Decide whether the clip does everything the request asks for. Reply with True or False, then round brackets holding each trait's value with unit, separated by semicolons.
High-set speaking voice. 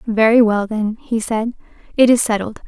True (225 Hz)